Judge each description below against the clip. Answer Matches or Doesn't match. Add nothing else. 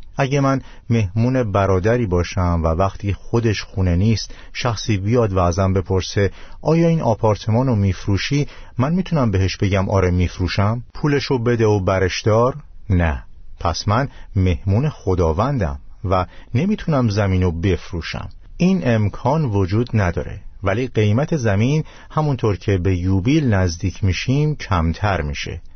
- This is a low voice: Matches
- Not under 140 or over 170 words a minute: Doesn't match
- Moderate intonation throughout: Matches